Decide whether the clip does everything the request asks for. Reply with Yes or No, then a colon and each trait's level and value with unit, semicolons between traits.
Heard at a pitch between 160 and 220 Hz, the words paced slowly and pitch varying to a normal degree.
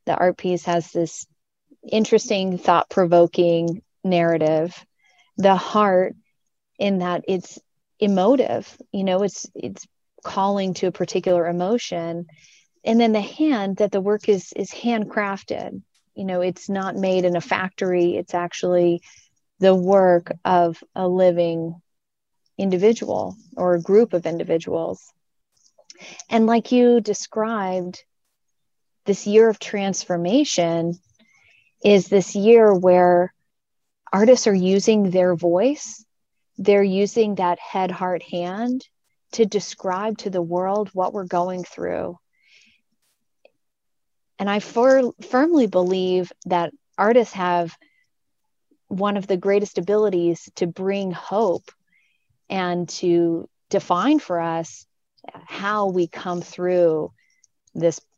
Yes: high, 190 Hz; slow, 115 wpm; average, 3.1 semitones